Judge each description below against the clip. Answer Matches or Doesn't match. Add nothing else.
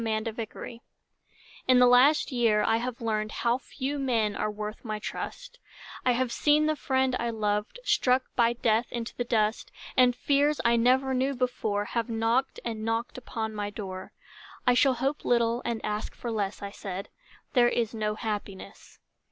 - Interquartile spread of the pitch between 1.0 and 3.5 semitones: Matches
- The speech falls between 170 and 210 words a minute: Matches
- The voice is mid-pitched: Doesn't match